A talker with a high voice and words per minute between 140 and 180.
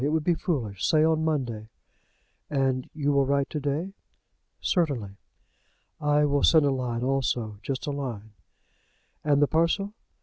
No: medium, 140 Hz; average, 155 wpm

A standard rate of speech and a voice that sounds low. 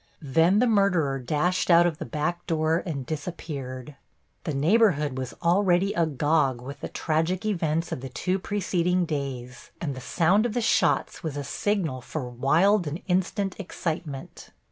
No: average, 160 wpm; medium, 160 Hz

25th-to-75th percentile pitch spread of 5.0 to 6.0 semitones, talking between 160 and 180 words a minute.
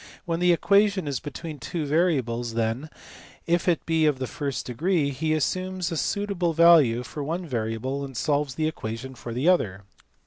Yes: average, 5.3 semitones; average, 175 wpm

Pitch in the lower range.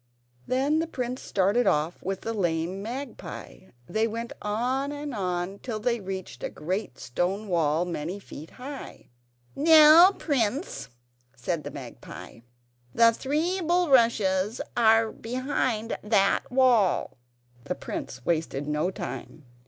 No: high, 220 Hz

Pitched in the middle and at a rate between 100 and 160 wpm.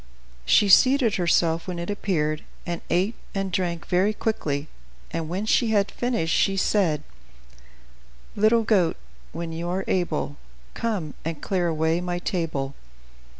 Yes: medium, 175 Hz; average, 140 wpm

